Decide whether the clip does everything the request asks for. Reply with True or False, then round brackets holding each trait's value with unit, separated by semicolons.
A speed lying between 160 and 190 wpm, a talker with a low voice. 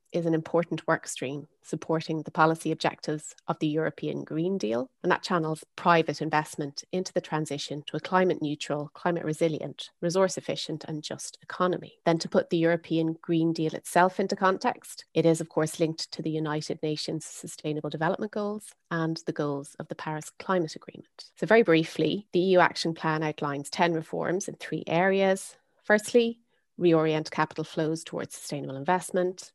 False (170 wpm; 165 Hz)